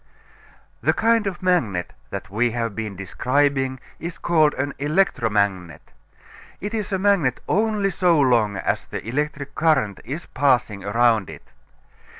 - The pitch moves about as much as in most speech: No, wide, 8.0 semitones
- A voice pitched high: No, low, 135 Hz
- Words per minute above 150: No, average, 140 wpm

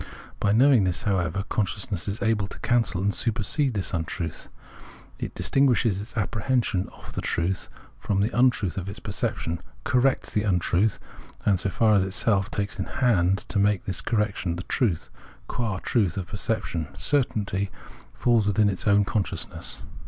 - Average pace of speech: Yes, average, 160 wpm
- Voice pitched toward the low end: Yes, low, 100 Hz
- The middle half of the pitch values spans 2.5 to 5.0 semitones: Yes, average, 3.1 semitones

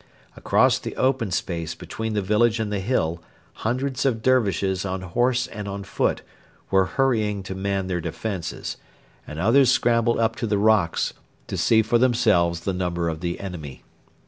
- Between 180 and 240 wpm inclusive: No, average, 165 wpm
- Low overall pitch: Yes, low, 100 Hz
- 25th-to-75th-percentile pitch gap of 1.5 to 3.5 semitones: No, average, 4.2 semitones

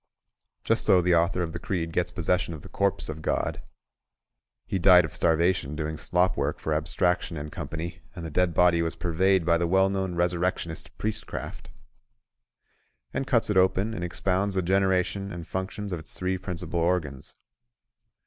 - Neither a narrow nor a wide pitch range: No, narrow, 2.2 semitones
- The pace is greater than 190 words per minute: No, average, 170 wpm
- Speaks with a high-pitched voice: No, very low, 90 Hz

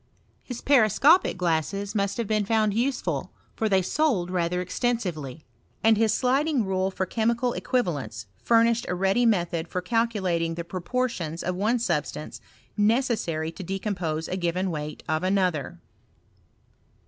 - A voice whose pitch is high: Yes, high, 195 Hz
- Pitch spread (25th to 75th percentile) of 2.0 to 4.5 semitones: No, average, 5.1 semitones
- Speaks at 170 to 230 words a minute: No, average, 140 wpm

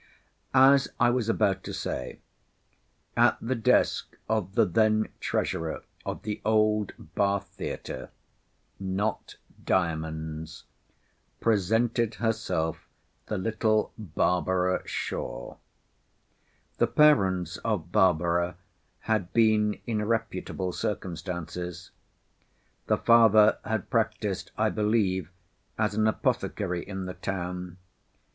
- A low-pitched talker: Yes, low, 100 Hz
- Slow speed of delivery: Yes, slow, 95 wpm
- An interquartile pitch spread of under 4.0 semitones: Yes, average, 3.5 semitones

